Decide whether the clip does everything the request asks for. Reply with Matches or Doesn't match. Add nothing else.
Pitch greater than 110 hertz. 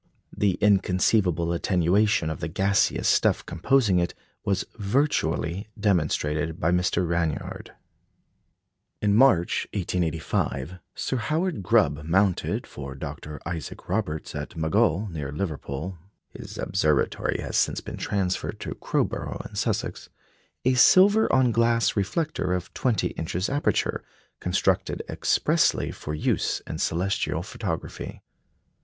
Doesn't match